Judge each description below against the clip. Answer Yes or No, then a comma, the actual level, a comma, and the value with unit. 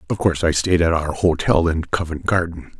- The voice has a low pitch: Yes, very low, 85 Hz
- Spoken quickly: Yes, fast, 215 wpm